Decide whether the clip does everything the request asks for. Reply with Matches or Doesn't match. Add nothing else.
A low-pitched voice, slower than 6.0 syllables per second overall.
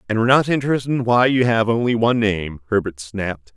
Doesn't match